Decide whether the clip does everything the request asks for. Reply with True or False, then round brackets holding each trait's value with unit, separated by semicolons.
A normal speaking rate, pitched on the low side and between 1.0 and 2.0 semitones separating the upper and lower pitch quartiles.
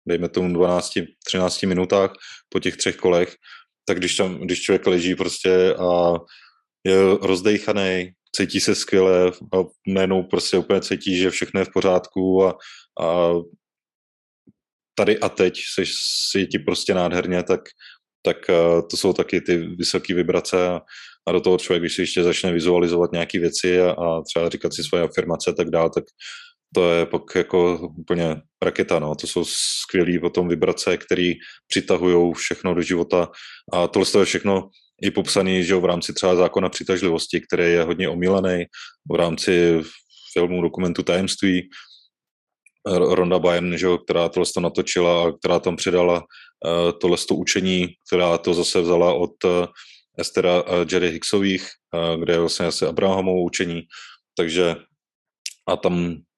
True (155 wpm; 90 Hz; 1.4 semitones)